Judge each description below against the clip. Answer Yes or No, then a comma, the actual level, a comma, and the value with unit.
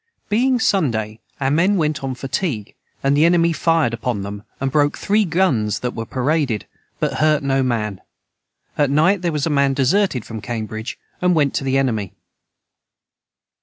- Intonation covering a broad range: Yes, wide, 5.9 semitones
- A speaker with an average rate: Yes, average, 165 wpm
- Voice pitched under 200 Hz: Yes, medium, 140 Hz